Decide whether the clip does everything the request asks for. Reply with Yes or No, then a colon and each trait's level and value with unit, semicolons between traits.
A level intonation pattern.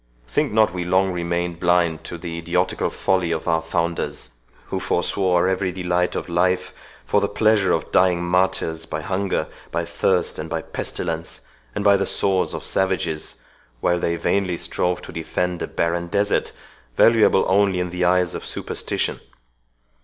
Yes: narrow, 1.7 semitones